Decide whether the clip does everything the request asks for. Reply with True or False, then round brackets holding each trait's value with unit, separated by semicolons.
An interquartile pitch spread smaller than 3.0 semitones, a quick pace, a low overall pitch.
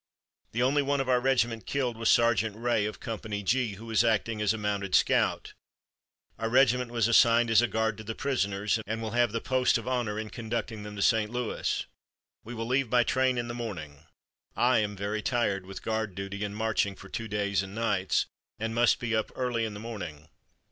True (2.5 semitones; 210 wpm; 115 Hz)